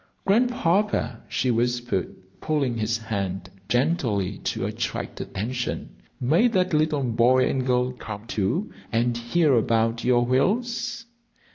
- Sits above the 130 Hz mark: No, low, 125 Hz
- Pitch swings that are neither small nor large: No, wide, 6.2 semitones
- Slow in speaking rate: Yes, slow, 120 wpm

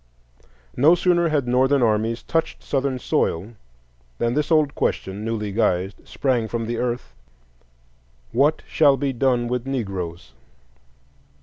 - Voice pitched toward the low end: Yes, low, 120 Hz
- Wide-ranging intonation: Yes, wide, 6.0 semitones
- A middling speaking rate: No, slow, 120 wpm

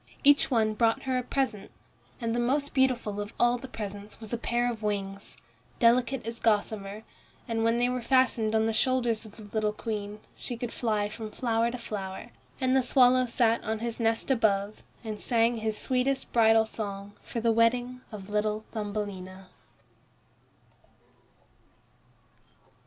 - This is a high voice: Yes, high, 225 Hz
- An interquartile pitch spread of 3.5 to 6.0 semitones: No, narrow, 2.4 semitones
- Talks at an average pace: Yes, average, 160 wpm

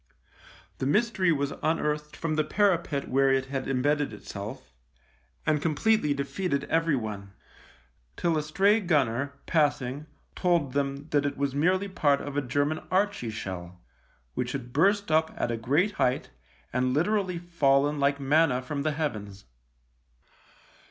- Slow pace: No, average, 155 wpm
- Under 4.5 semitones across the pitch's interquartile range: Yes, average, 3.7 semitones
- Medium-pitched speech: Yes, medium, 145 Hz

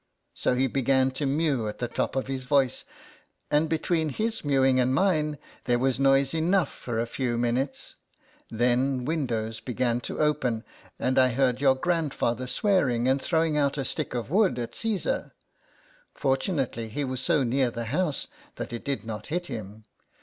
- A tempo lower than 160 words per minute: No, average, 170 wpm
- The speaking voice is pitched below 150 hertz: Yes, low, 135 Hz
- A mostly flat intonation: No, average, 3.7 semitones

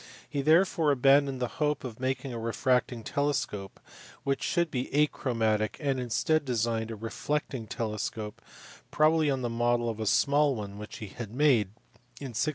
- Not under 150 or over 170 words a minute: Yes, average, 165 wpm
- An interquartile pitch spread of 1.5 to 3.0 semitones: No, average, 4.2 semitones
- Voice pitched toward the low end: Yes, low, 125 Hz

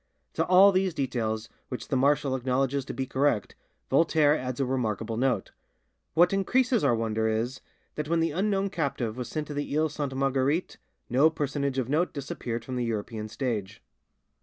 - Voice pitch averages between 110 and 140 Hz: Yes, low, 135 Hz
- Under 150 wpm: No, average, 175 wpm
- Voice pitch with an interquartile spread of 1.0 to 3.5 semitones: No, average, 4.2 semitones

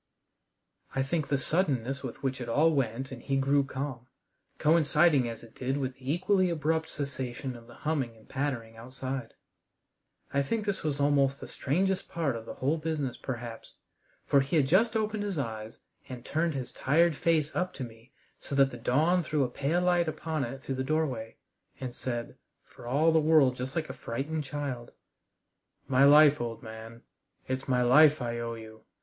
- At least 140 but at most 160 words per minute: No, average, 185 wpm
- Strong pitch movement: No, average, 4.0 semitones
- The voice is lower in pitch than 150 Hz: Yes, low, 135 Hz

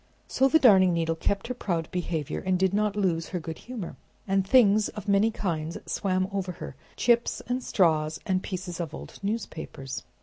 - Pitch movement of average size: Yes, average, 4.0 semitones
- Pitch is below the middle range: No, medium, 185 Hz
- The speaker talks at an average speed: Yes, average, 180 wpm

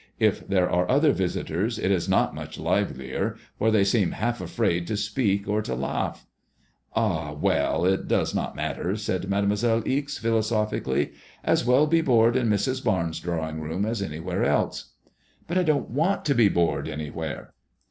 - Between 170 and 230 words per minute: Yes, average, 175 wpm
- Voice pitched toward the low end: Yes, low, 100 Hz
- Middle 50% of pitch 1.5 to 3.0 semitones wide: No, average, 5.3 semitones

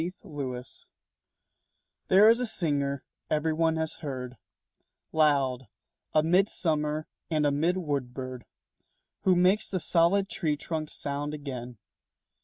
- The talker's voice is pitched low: No, medium, 155 Hz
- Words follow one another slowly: Yes, slow, 130 wpm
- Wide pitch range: No, average, 3.6 semitones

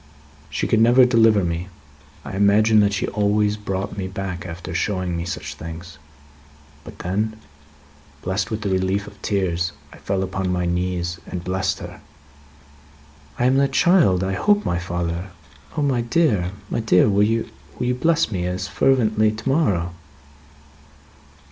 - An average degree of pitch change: Yes, average, 3.7 semitones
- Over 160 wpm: No, average, 155 wpm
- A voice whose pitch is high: No, very low, 95 Hz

